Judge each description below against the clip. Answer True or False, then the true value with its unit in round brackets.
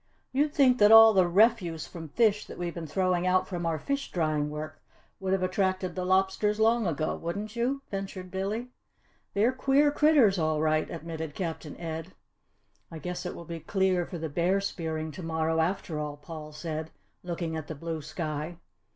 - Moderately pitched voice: True (175 Hz)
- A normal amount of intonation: True (3.8 semitones)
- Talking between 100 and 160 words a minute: False (185 wpm)